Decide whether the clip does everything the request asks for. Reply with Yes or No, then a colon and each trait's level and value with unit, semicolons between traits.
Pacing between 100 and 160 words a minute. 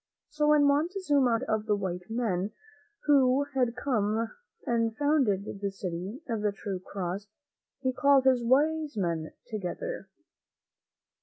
Yes: slow, 135 wpm